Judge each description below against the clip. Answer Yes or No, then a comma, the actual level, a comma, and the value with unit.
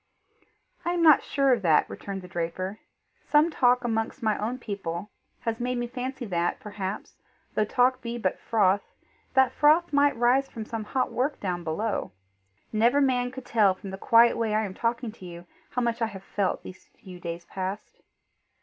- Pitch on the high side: Yes, high, 225 Hz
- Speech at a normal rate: Yes, average, 185 wpm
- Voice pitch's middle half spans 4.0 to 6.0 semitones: Yes, average, 4.5 semitones